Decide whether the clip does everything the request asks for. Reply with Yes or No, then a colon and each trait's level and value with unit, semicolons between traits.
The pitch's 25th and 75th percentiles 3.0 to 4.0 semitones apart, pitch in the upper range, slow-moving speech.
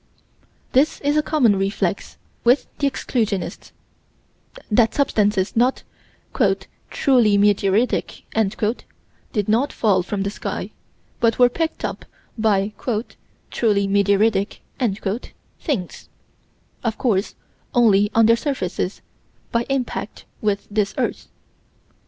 Yes: average, 3.5 semitones; high, 215 Hz; slow, 105 wpm